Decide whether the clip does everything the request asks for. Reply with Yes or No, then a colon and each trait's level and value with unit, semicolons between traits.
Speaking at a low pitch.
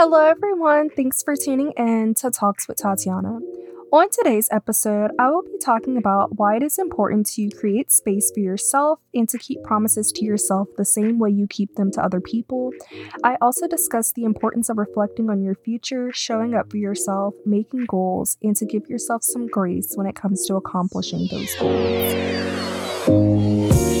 No: high, 215 Hz